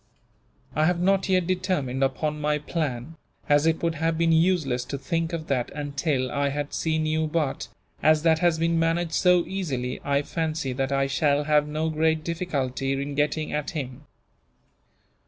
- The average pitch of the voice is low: No, medium, 155 Hz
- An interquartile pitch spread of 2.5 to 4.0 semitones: Yes, average, 2.8 semitones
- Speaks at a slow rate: No, average, 175 wpm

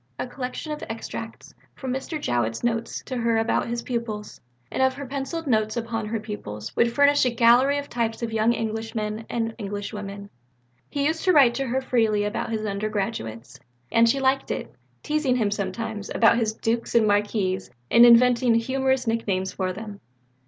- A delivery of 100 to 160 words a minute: No, average, 185 wpm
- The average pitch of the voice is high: Yes, high, 230 Hz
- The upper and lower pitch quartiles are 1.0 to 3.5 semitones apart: Yes, average, 3.1 semitones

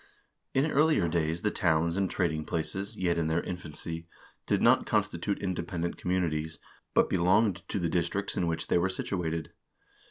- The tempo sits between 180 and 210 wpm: No, average, 160 wpm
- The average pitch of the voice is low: Yes, very low, 85 Hz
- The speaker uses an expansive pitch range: No, narrow, 2.5 semitones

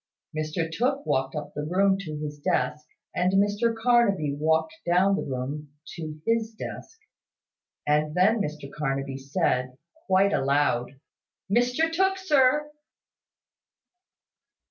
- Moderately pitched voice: Yes, medium, 165 Hz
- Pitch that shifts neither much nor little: No, wide, 7.1 semitones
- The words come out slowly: Yes, slow, 120 wpm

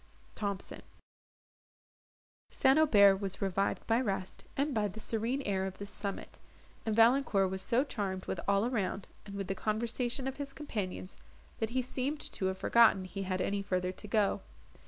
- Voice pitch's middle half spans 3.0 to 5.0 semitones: Yes, average, 3.8 semitones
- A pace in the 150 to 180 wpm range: Yes, average, 170 wpm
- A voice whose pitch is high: Yes, high, 205 Hz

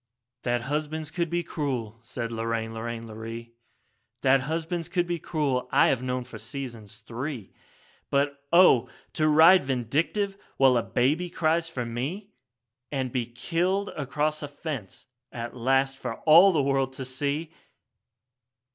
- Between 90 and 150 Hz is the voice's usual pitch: Yes, low, 135 Hz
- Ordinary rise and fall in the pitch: Yes, average, 4.7 semitones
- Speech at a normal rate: Yes, average, 145 wpm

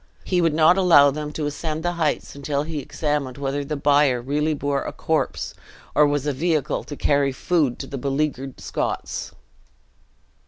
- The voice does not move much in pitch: Yes, narrow, 1.8 semitones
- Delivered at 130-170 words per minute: No, average, 180 wpm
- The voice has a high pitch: No, medium, 145 Hz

